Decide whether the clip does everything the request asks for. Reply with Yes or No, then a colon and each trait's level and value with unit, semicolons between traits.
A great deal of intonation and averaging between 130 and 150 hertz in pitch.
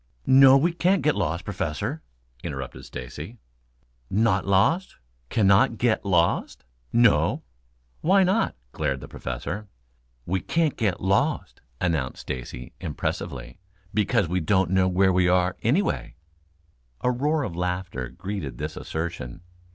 No: wide, 6.9 semitones; very low, 95 Hz